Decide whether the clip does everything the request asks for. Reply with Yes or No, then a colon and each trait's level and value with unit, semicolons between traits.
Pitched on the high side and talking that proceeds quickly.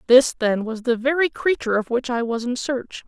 Yes: very high, 250 Hz; fast, 235 wpm